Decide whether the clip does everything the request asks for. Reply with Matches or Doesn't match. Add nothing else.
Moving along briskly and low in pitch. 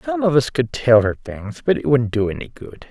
Matches